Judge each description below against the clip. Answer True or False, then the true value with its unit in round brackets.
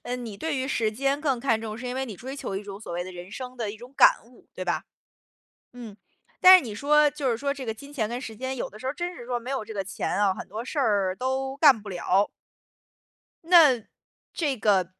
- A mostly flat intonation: False (4.5 semitones)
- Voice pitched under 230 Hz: False (245 Hz)